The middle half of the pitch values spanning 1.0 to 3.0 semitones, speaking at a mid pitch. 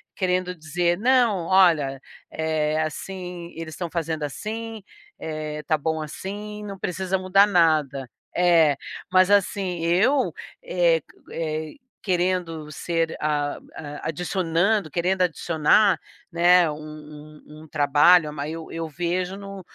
No: average, 3.4 semitones; medium, 170 Hz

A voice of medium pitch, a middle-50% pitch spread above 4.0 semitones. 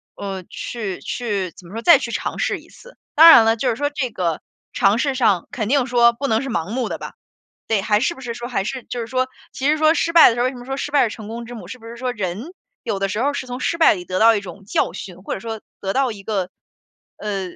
No: high, 230 Hz; average, 4.5 semitones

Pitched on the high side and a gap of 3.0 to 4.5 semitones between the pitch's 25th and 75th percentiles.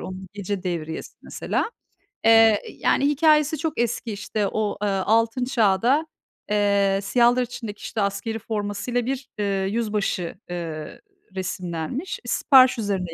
Yes: high, 210 Hz; average, 3.9 semitones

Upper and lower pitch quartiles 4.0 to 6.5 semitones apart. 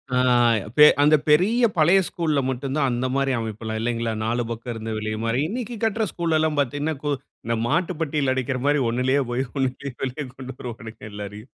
Yes: average, 4.7 semitones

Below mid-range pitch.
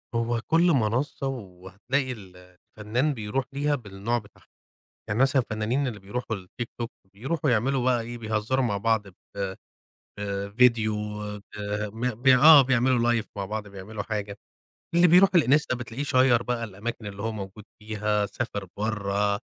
Yes: low, 115 Hz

